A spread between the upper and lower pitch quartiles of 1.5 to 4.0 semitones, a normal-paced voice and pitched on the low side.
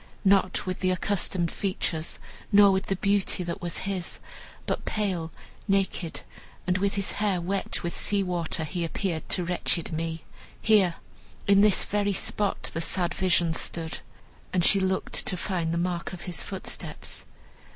No: narrow, 2.5 semitones; average, 160 wpm; medium, 185 Hz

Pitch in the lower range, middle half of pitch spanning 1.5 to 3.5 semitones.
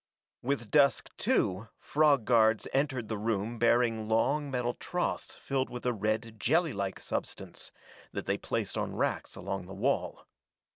No: low, 120 Hz; average, 4.1 semitones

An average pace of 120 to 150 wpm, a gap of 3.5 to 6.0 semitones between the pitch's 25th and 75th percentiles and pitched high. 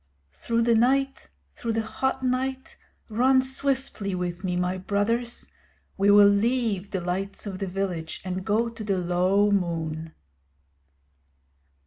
Yes: slow, 135 wpm; average, 4.4 semitones; high, 205 Hz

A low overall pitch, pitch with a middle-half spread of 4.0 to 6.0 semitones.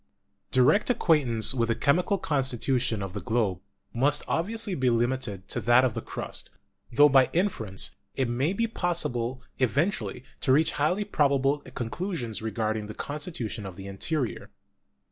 Yes: low, 130 Hz; average, 5.1 semitones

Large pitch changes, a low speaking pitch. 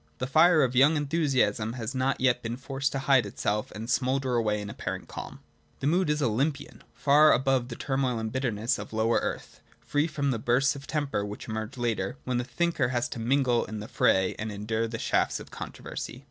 No: average, 3.6 semitones; low, 125 Hz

